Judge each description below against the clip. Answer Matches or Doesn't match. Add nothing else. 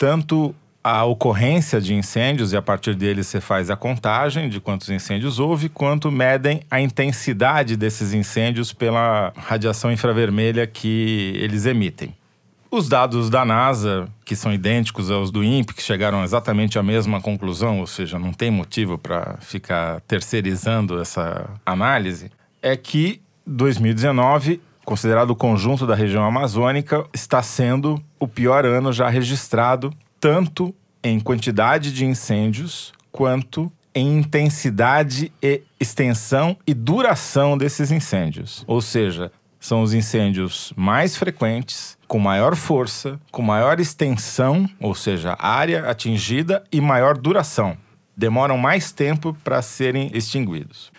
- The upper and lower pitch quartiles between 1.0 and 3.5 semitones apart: Doesn't match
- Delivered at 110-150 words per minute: Matches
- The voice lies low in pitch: Matches